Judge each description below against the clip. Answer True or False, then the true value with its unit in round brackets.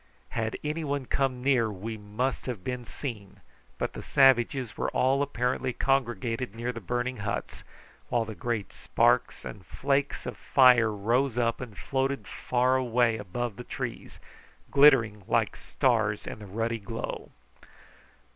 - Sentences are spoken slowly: False (145 wpm)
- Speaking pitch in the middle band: False (120 Hz)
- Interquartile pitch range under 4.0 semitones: True (2.9 semitones)